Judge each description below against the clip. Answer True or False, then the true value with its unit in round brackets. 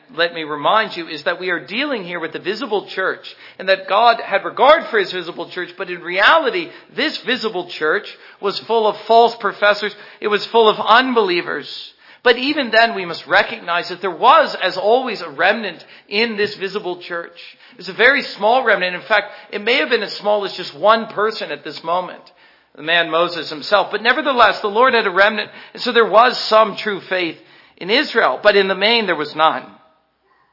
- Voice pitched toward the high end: True (205 Hz)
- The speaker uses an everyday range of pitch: True (4.4 semitones)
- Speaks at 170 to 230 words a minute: True (205 wpm)